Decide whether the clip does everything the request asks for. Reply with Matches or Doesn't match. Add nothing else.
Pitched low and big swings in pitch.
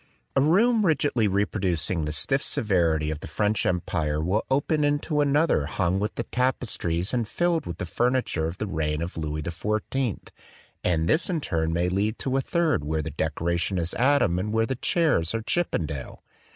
Matches